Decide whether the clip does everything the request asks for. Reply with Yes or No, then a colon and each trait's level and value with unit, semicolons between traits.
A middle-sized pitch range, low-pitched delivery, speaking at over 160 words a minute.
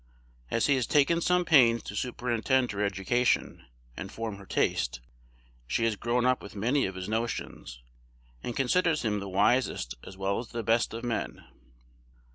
Yes: average, 4.0 semitones; low, 115 Hz; average, 170 wpm